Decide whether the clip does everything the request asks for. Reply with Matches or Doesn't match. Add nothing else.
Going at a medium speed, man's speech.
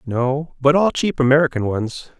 Matches